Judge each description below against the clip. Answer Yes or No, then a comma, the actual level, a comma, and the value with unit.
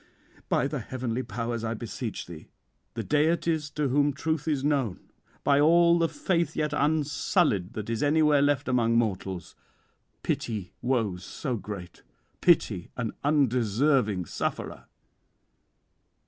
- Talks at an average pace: No, slow, 125 wpm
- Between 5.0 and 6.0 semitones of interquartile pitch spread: Yes, average, 5.3 semitones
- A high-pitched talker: No, low, 130 Hz